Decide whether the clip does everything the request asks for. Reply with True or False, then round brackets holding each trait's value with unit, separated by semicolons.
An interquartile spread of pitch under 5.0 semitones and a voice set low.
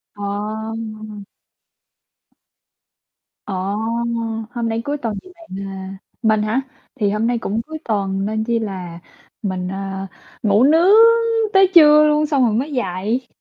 False (4.3 semitones; 220 Hz)